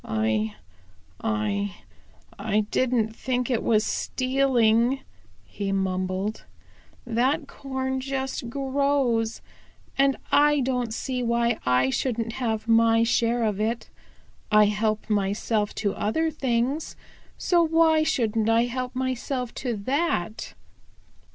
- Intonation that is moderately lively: Yes, average, 3.5 semitones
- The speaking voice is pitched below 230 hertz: No, high, 235 Hz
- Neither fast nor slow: No, slow, 110 wpm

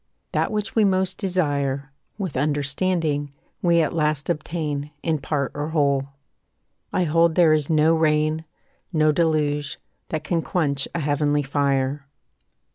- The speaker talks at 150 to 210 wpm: No, slow, 135 wpm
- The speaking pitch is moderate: Yes, medium, 150 Hz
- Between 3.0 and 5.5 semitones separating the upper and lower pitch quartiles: No, narrow, 2.6 semitones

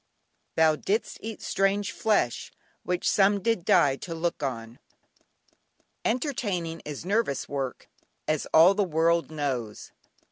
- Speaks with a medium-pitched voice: Yes, medium, 170 Hz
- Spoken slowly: Yes, slow, 120 wpm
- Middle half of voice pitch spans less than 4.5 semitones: No, wide, 5.6 semitones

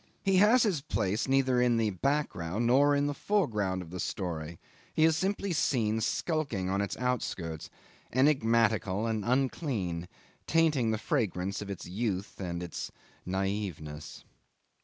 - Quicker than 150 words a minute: No, average, 145 wpm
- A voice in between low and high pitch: No, low, 110 Hz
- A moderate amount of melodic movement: No, wide, 7.2 semitones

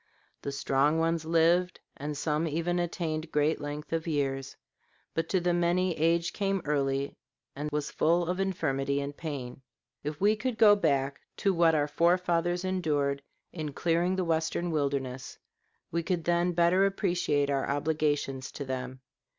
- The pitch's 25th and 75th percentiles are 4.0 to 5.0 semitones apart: No, average, 3.5 semitones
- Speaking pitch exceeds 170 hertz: No, medium, 160 Hz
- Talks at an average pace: Yes, average, 160 wpm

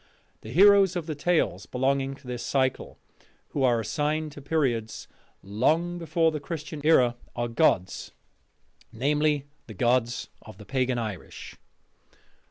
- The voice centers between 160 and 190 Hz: No, low, 135 Hz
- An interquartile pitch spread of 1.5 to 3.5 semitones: No, average, 4.6 semitones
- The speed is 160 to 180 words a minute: No, slow, 135 wpm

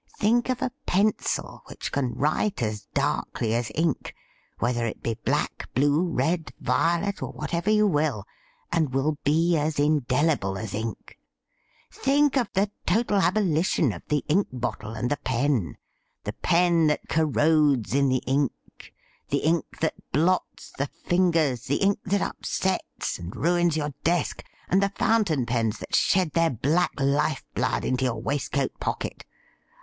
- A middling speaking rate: Yes, average, 160 wpm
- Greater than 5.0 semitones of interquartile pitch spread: Yes, wide, 5.5 semitones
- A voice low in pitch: No, medium, 150 Hz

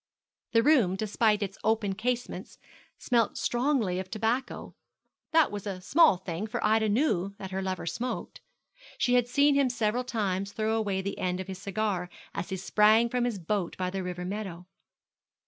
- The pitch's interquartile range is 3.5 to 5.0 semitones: Yes, average, 3.8 semitones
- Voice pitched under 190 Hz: No, high, 210 Hz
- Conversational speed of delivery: Yes, average, 175 wpm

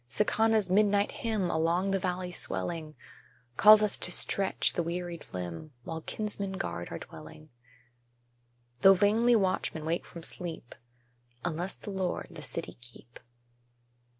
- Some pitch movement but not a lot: Yes, average, 3.9 semitones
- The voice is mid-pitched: Yes, medium, 180 Hz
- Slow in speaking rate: Yes, slow, 130 wpm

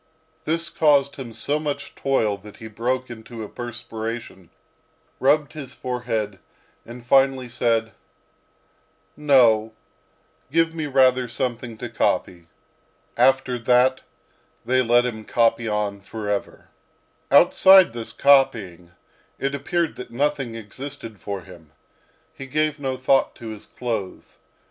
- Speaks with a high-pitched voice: No, low, 125 Hz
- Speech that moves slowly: Yes, slow, 120 wpm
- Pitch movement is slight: No, average, 3.6 semitones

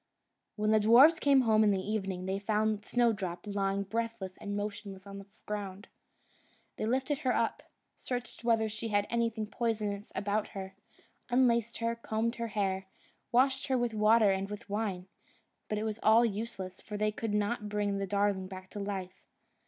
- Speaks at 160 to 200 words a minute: Yes, average, 170 wpm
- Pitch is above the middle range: Yes, high, 210 Hz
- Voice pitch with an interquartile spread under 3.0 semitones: Yes, narrow, 2.6 semitones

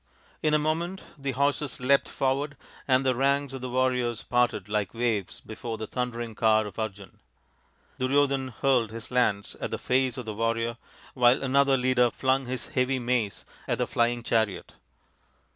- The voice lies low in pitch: Yes, low, 125 Hz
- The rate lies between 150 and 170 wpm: Yes, average, 165 wpm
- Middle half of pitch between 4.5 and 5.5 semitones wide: No, average, 2.8 semitones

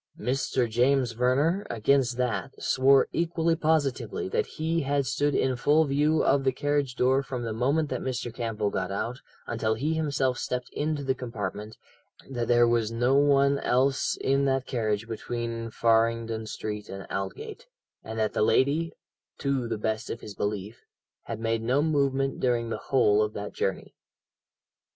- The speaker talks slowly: No, average, 165 wpm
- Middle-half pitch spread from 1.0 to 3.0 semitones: No, average, 3.6 semitones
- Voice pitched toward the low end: Yes, low, 125 Hz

